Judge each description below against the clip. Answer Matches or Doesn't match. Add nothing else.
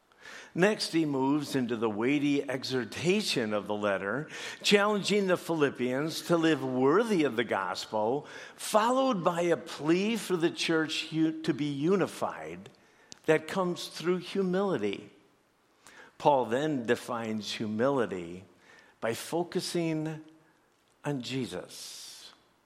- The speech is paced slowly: Matches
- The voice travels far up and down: Matches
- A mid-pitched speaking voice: Matches